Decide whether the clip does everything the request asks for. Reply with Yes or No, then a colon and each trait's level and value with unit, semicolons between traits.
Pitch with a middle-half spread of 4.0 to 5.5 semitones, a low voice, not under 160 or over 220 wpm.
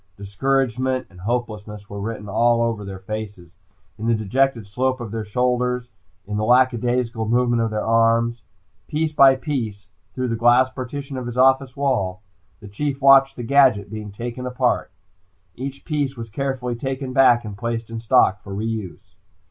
No: average, 3.3 semitones; low, 120 Hz; average, 170 wpm